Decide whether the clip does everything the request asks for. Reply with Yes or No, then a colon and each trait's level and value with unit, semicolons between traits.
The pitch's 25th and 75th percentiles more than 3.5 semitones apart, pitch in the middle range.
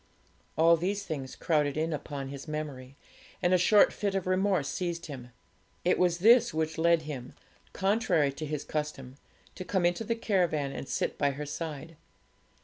Yes: average, 4.2 semitones; medium, 160 Hz